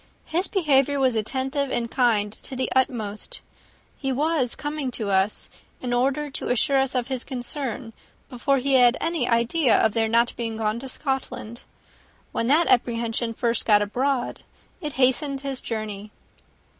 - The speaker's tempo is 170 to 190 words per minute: No, average, 155 wpm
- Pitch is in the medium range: No, very high, 255 Hz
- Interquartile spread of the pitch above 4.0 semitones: No, average, 3.1 semitones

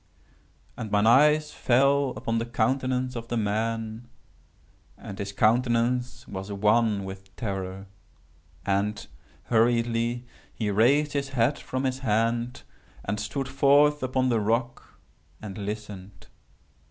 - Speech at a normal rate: No, slow, 120 wpm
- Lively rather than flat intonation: No, average, 3.5 semitones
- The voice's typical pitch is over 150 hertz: No, low, 115 Hz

